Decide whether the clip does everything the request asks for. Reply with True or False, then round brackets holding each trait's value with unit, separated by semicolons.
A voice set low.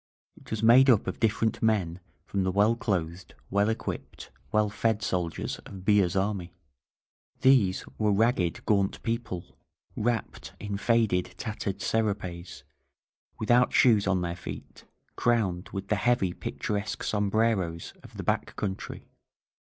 True (105 Hz)